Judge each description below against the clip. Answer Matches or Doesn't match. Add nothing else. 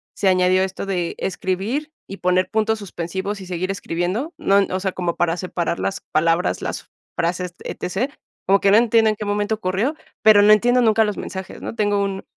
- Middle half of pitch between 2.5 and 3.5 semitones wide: Matches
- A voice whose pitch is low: Doesn't match